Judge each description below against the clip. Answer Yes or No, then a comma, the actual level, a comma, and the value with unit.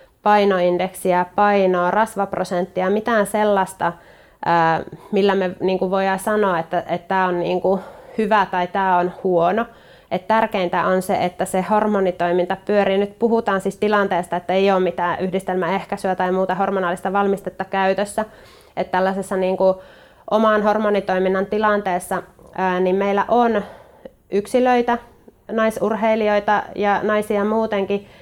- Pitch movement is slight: Yes, narrow, 2.2 semitones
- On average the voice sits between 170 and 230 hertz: Yes, high, 190 Hz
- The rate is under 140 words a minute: Yes, average, 110 wpm